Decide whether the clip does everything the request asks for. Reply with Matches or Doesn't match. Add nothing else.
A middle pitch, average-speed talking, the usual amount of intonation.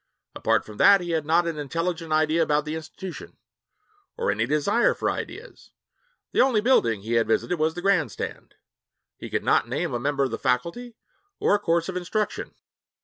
Matches